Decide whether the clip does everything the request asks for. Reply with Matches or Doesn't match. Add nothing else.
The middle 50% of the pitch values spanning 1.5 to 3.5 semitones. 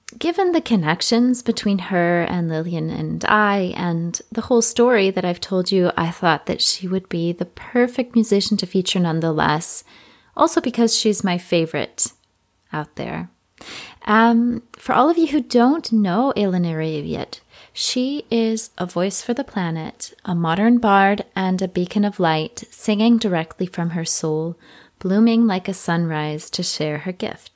Doesn't match